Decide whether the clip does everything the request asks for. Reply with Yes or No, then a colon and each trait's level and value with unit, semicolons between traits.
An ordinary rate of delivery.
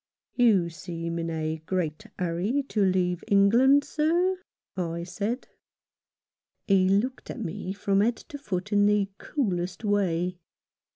No: slow, 130 wpm